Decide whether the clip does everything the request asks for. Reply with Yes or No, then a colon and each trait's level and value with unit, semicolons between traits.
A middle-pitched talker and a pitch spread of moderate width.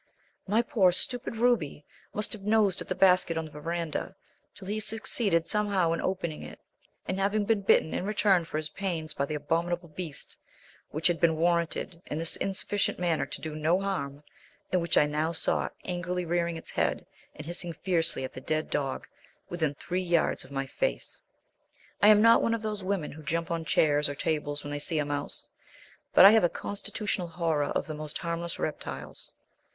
Yes: medium, 170 Hz; average, 3.9 semitones